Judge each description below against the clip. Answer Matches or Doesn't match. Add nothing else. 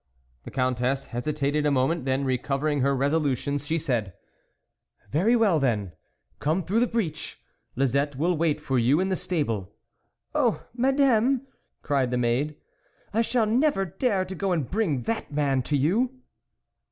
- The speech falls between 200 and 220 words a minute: Doesn't match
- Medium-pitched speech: Matches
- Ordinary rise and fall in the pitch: Doesn't match